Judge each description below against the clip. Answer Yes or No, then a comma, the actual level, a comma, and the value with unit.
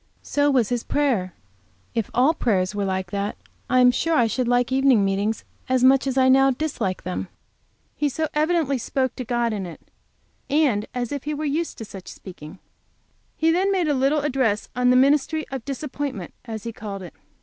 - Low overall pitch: No, very high, 255 Hz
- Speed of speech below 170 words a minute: No, average, 195 wpm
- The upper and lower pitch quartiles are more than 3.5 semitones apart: Yes, average, 5.3 semitones